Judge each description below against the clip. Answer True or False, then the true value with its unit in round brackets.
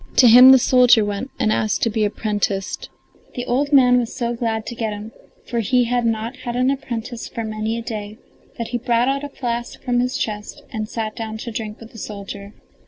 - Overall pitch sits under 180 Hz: False (230 Hz)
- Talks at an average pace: False (220 wpm)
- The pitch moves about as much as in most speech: False (2.3 semitones)